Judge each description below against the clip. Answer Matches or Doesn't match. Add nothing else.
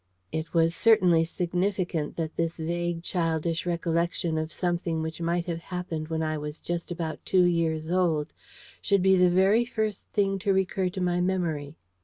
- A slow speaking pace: Doesn't match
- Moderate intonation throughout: Doesn't match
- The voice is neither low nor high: Matches